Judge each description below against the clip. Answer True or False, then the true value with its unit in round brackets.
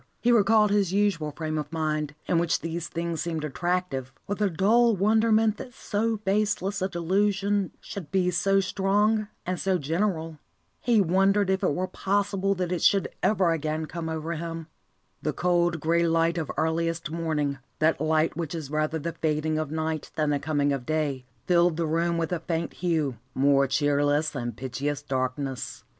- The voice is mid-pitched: True (165 Hz)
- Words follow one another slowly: False (175 wpm)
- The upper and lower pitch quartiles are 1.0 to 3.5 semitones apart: False (3.9 semitones)